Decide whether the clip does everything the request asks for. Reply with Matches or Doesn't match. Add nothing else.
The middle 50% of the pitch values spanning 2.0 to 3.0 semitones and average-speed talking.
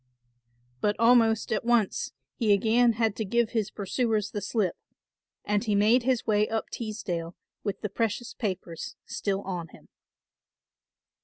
Matches